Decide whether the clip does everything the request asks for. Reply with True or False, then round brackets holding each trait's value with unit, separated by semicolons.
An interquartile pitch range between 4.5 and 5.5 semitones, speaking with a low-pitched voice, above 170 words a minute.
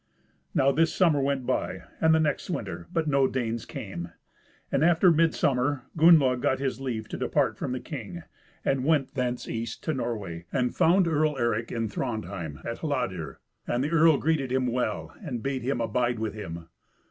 True (4.8 semitones; 130 Hz; 180 wpm)